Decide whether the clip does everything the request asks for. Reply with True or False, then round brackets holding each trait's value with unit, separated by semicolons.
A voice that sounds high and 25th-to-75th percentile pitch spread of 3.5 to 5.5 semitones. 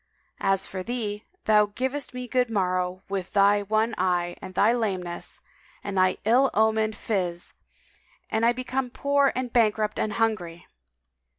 True (215 Hz; 4.2 semitones)